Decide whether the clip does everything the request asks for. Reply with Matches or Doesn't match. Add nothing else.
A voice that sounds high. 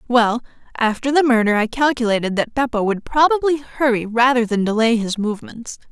Matches